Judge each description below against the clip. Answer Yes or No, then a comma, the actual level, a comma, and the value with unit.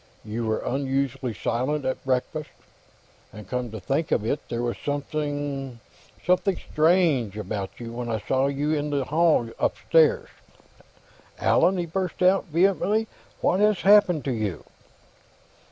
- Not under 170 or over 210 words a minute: No, average, 140 wpm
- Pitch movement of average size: No, wide, 5.8 semitones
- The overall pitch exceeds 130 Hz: Yes, medium, 140 Hz